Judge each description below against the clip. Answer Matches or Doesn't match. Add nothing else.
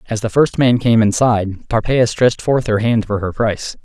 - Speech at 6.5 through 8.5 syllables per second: Doesn't match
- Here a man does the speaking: Matches